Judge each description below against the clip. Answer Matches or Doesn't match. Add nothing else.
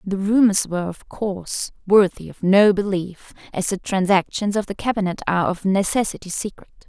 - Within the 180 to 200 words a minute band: Doesn't match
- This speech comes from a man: Doesn't match